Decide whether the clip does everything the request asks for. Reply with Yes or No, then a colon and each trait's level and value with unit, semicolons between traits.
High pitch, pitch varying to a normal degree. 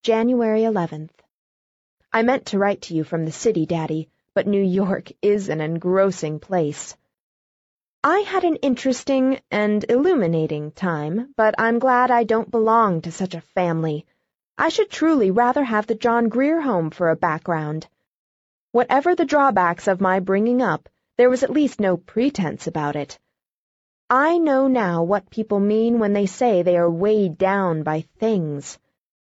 No: high, 205 Hz; wide, 6.5 semitones